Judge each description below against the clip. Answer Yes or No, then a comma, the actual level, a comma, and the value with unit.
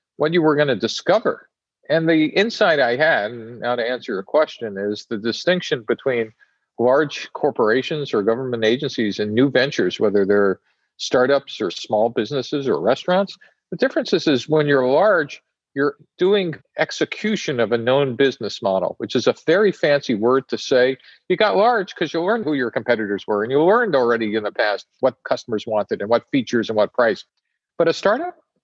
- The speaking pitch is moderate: No, low, 130 Hz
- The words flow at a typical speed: Yes, average, 185 wpm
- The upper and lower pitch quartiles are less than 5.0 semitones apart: No, wide, 5.6 semitones